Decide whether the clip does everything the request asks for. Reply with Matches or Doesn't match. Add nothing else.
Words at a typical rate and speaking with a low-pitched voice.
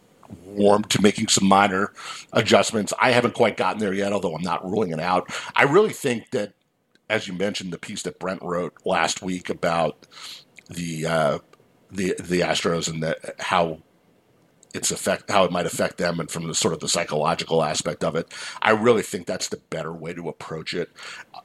Matches